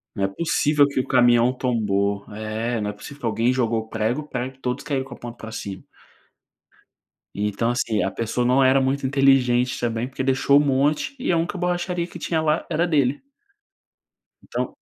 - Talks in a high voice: No, low, 125 Hz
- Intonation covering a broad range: No, average, 3.8 semitones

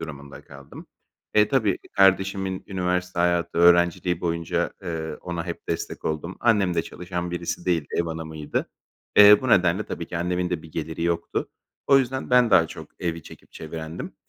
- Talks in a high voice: No, very low, 85 Hz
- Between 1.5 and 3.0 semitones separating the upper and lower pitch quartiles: Yes, narrow, 2.4 semitones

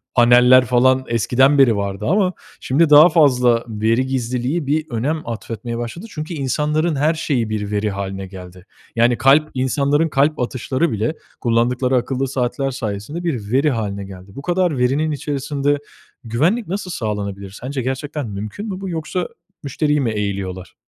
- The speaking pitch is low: Yes, low, 130 Hz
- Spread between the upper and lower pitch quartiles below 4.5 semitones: No, average, 5.0 semitones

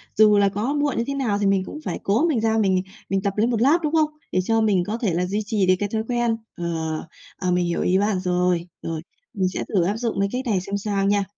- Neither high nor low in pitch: No, high, 205 Hz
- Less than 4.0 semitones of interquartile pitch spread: Yes, average, 3.4 semitones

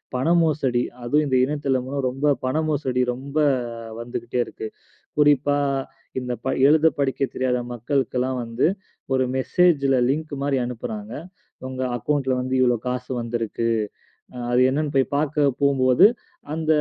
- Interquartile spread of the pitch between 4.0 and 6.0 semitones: No, narrow, 2.6 semitones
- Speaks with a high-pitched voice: No, low, 130 Hz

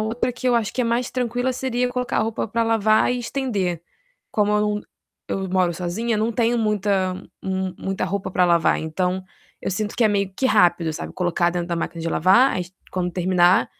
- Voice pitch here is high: Yes, high, 205 Hz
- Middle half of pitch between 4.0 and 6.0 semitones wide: Yes, average, 4.4 semitones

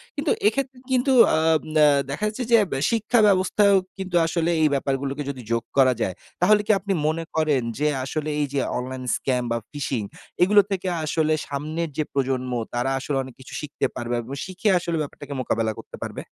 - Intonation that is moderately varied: No, wide, 6.0 semitones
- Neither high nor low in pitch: Yes, medium, 155 Hz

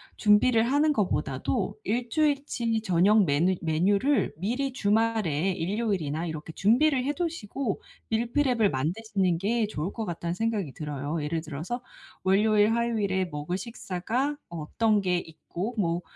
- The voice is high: Yes, high, 205 Hz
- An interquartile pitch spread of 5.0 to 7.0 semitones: Yes, wide, 5.5 semitones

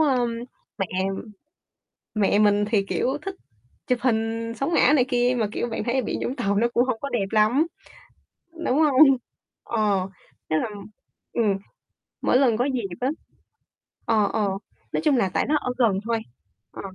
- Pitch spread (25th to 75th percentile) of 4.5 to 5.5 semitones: No, average, 3.7 semitones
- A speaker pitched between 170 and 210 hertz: No, high, 235 Hz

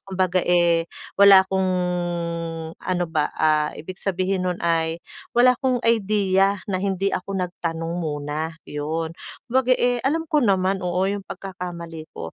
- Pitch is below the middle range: No, medium, 185 Hz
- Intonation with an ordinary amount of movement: Yes, average, 3.0 semitones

